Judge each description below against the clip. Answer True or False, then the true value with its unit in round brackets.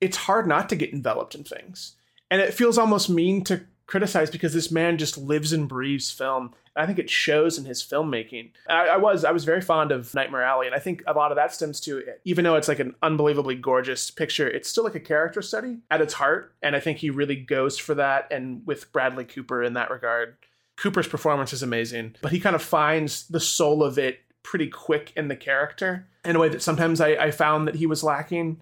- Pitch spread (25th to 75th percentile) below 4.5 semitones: True (3.4 semitones)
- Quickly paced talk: True (235 wpm)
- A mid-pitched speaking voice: True (150 Hz)